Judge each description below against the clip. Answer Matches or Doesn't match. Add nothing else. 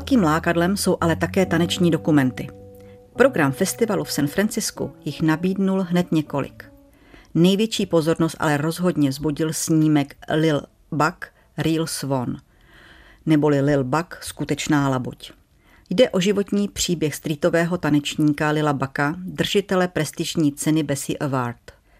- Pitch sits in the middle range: Matches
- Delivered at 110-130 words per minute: Matches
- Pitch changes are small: Doesn't match